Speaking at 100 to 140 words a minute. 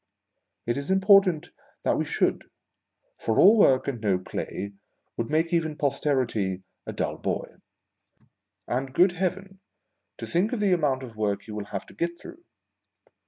No: average, 165 wpm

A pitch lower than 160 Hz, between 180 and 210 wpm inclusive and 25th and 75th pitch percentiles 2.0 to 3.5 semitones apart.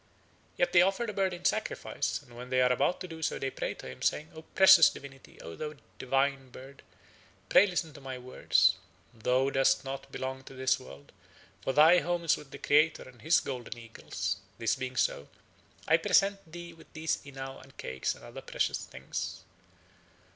No: low, 135 Hz; average, 190 wpm; average, 4.4 semitones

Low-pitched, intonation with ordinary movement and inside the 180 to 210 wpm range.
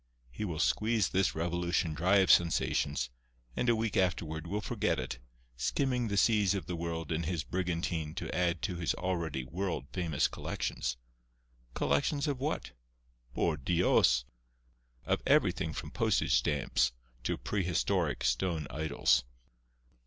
No: very low, 85 Hz; average, 3.7 semitones; average, 140 wpm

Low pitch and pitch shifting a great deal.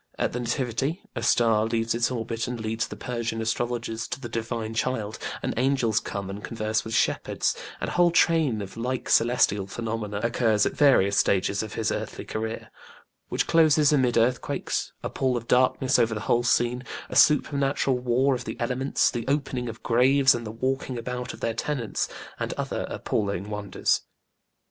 No: low, 120 Hz; narrow, 2.5 semitones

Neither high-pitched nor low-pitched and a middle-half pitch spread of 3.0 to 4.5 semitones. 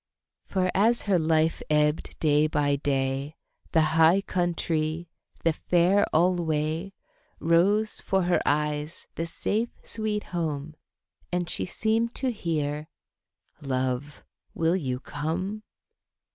Yes: medium, 165 Hz; average, 3.6 semitones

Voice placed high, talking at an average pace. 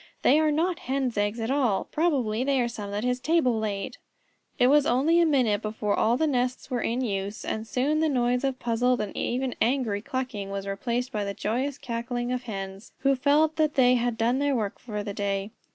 No: high, 245 Hz; fast, 215 wpm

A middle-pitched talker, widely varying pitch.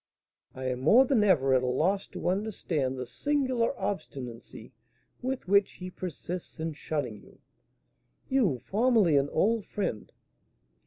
Yes: medium, 180 Hz; wide, 8.6 semitones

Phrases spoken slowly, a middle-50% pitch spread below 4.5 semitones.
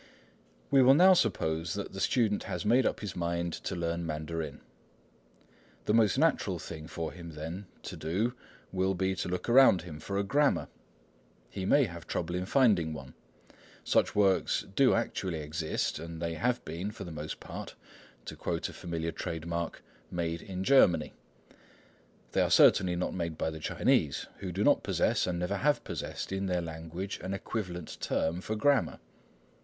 No: average, 175 wpm; average, 3.8 semitones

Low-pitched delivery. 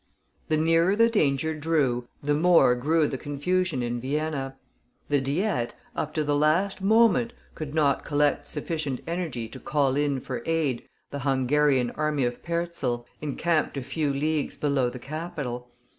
No: medium, 145 Hz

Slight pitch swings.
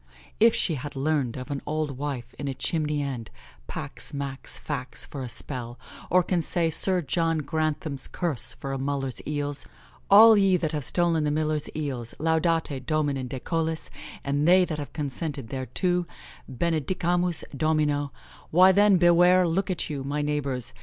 No: average, 3.6 semitones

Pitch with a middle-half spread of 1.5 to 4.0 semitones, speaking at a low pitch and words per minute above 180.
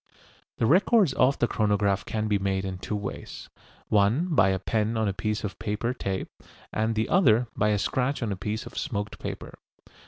Yes: average, 3.0 semitones; low, 105 Hz; average, 195 wpm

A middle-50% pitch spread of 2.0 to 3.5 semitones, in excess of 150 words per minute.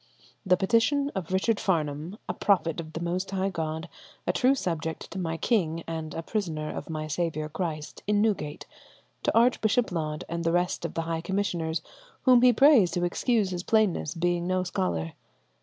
No: average, 4.1 semitones; average, 180 wpm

